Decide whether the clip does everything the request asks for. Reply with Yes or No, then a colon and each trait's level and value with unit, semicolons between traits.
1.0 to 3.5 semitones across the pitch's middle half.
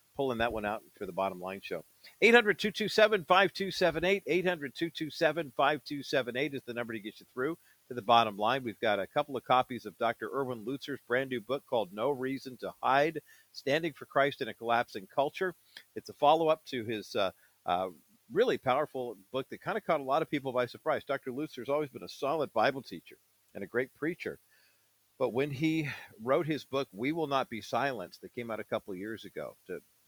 No: average, 4.6 semitones